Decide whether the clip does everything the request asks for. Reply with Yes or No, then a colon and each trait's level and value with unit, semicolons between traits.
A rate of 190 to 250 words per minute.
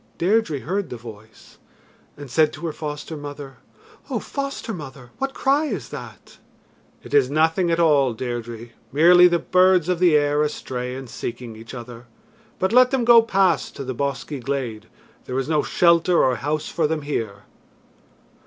No: average, 170 wpm